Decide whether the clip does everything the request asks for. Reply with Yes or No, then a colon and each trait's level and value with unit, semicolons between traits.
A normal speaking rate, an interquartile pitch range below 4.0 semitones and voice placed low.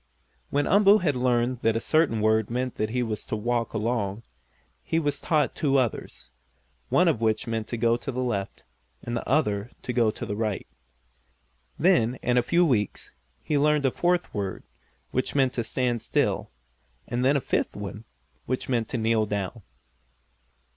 Yes: average, 180 wpm; average, 3.5 semitones; low, 120 Hz